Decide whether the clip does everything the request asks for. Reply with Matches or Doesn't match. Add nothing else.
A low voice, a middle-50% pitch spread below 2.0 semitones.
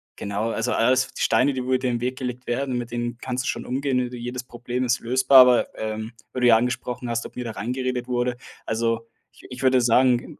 Matches